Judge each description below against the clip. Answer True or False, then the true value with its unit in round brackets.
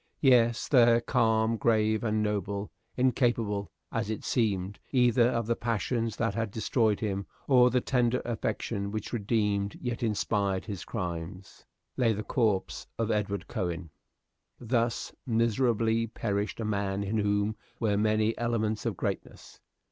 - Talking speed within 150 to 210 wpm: False (140 wpm)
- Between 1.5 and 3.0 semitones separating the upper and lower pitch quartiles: True (2.4 semitones)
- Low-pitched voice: True (110 Hz)